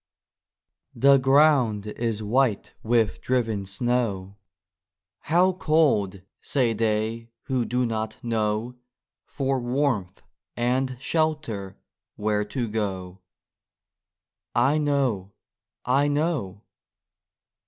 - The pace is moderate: No, slow, 90 wpm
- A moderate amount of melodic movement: Yes, average, 4.6 semitones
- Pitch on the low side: Yes, low, 115 Hz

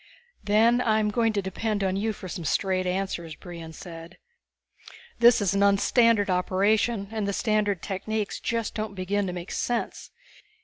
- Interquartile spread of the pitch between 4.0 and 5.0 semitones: No, average, 2.8 semitones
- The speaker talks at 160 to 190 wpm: Yes, average, 165 wpm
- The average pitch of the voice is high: Yes, high, 200 Hz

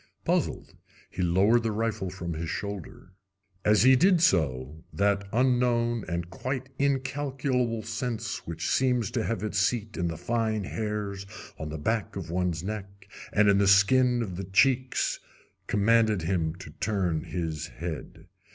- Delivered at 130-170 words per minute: Yes, average, 150 wpm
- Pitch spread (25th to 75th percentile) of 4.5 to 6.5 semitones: Yes, average, 4.8 semitones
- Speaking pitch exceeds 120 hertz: No, low, 105 Hz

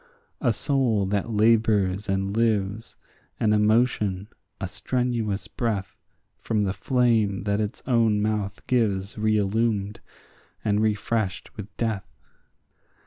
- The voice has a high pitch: No, low, 105 Hz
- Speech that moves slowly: Yes, slow, 110 wpm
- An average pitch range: No, narrow, 2.3 semitones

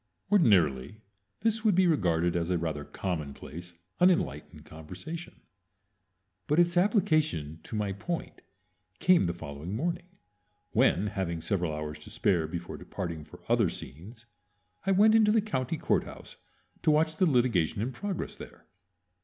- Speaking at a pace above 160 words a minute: No, average, 140 wpm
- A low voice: Yes, low, 105 Hz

